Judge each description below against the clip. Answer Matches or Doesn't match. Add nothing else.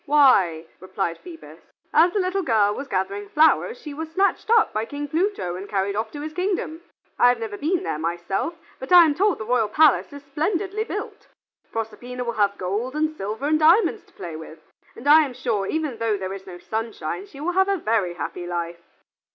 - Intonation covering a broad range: Matches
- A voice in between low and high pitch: Doesn't match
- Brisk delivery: Matches